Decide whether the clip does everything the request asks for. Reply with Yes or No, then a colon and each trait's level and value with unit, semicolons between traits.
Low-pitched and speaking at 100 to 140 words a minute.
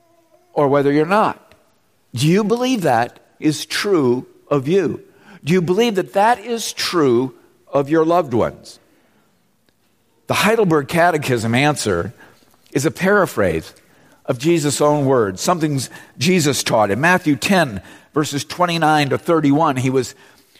No: medium, 155 Hz; slow, 135 wpm